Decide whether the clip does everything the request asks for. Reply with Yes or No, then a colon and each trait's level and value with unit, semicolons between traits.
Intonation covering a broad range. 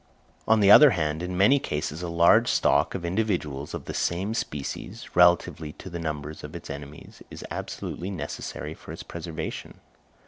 No: average, 4.1 semitones